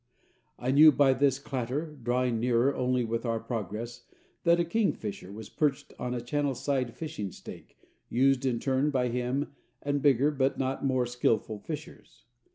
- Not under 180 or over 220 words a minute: No, average, 165 wpm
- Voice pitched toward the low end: Yes, low, 130 Hz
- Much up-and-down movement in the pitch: No, average, 3.1 semitones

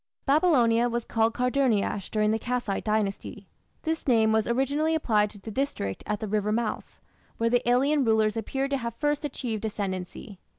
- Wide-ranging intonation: No, average, 4.0 semitones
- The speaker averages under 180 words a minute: Yes, average, 170 wpm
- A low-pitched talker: No, high, 230 Hz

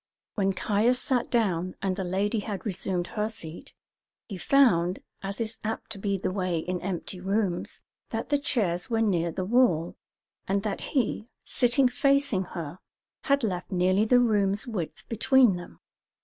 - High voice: Yes, high, 200 Hz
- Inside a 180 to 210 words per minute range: No, average, 165 wpm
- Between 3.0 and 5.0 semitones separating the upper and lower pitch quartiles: Yes, average, 4.0 semitones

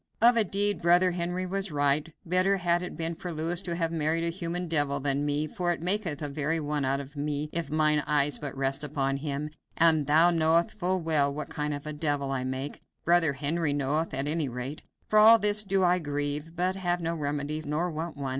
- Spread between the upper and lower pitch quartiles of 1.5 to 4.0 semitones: Yes, average, 3.3 semitones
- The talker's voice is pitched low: No, medium, 155 Hz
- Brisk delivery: Yes, fast, 220 wpm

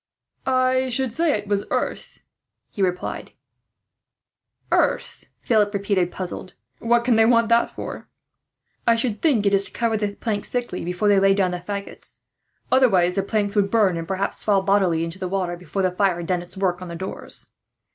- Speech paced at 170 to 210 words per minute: Yes, average, 185 wpm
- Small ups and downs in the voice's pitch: No, average, 3.7 semitones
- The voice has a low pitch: No, high, 200 Hz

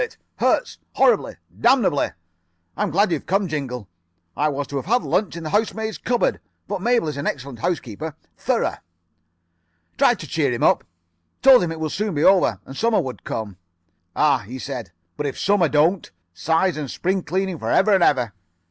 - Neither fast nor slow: Yes, average, 185 wpm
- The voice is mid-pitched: Yes, medium, 165 Hz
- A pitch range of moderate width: No, wide, 6.2 semitones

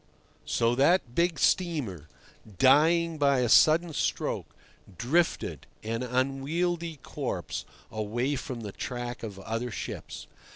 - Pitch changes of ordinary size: No, wide, 5.8 semitones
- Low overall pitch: Yes, low, 130 Hz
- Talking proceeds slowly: Yes, slow, 115 wpm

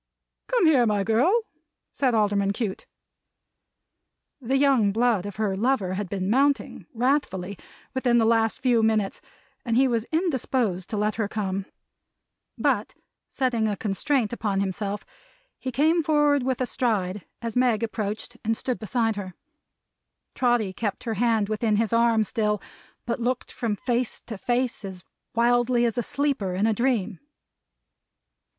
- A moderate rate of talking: Yes, average, 150 wpm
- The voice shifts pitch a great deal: No, average, 3.4 semitones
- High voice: Yes, high, 225 Hz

